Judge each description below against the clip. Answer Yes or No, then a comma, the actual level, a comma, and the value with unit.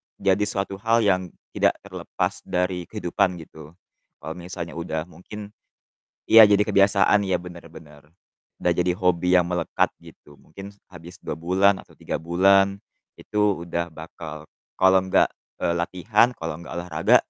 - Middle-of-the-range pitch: No, very low, 90 Hz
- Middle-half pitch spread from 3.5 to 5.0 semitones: No, narrow, 2.6 semitones